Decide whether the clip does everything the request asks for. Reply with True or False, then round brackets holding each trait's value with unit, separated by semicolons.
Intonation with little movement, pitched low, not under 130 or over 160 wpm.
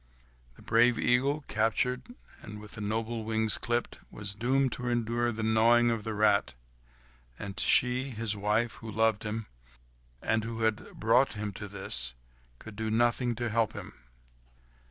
True (2.0 semitones; 110 Hz; 155 wpm)